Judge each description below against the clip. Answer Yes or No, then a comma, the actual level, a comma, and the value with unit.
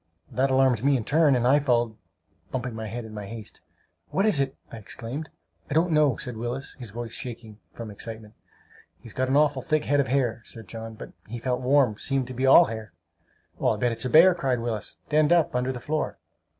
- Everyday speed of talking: No, fast, 220 wpm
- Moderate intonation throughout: Yes, average, 3.6 semitones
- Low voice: Yes, low, 125 Hz